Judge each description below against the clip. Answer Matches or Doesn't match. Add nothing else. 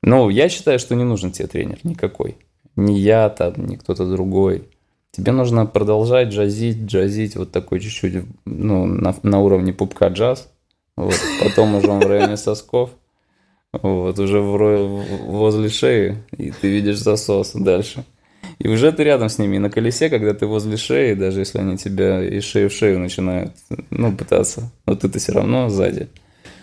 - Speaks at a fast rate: Matches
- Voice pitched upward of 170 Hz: Doesn't match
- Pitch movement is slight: Matches